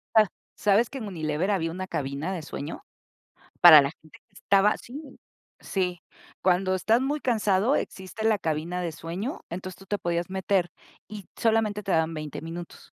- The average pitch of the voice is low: No, medium, 185 Hz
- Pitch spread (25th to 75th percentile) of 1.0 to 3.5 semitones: No, average, 4.0 semitones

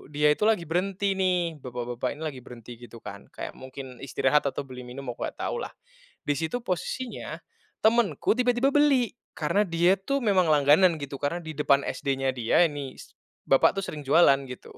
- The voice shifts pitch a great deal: Yes, wide, 6.4 semitones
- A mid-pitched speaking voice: Yes, medium, 150 Hz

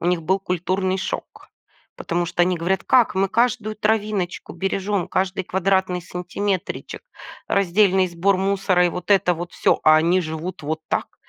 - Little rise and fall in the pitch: Yes, narrow, 2.0 semitones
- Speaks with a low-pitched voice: No, medium, 185 Hz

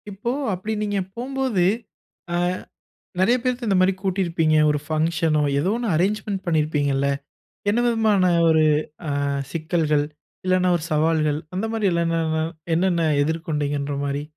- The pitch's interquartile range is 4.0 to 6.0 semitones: Yes, average, 4.5 semitones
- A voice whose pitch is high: No, medium, 170 Hz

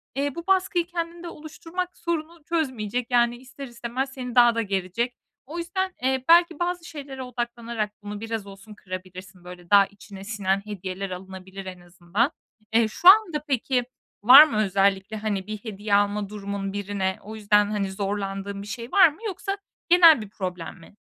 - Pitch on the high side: Yes, high, 220 Hz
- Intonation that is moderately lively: No, wide, 6.6 semitones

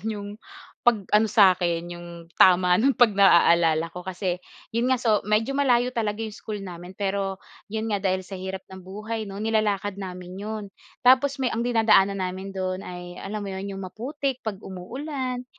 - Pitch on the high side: Yes, high, 200 Hz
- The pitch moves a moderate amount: Yes, average, 3.3 semitones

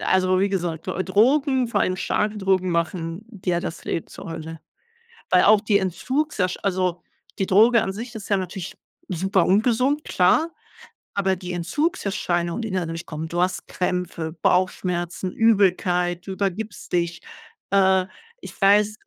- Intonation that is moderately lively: Yes, average, 3.0 semitones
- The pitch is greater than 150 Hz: Yes, high, 190 Hz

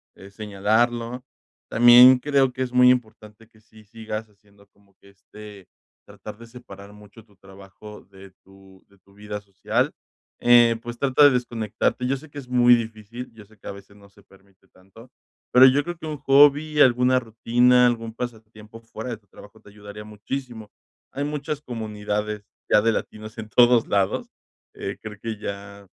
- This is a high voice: No, low, 110 Hz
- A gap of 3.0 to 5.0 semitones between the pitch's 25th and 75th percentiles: Yes, average, 3.3 semitones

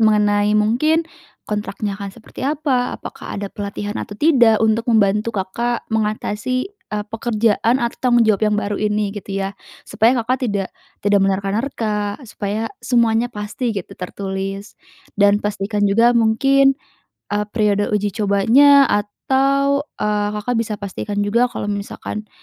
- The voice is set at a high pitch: Yes, high, 210 Hz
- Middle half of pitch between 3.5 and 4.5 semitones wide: No, average, 2.8 semitones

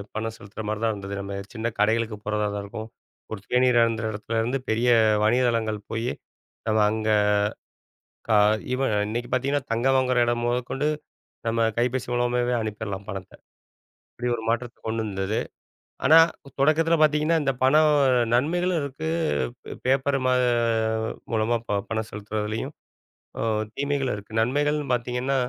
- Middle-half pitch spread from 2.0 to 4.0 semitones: Yes, average, 3.4 semitones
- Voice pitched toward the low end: Yes, low, 120 Hz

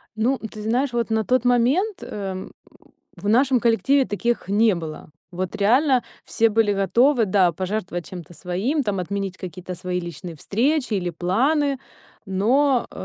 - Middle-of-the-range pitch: No, high, 215 Hz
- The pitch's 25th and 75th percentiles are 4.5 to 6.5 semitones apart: Yes, average, 5.2 semitones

